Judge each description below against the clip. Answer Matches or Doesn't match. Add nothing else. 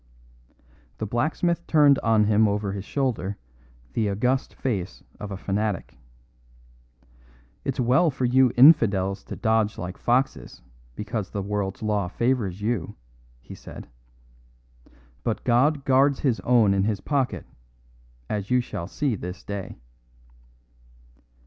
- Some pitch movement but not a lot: Matches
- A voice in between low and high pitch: Doesn't match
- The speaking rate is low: Matches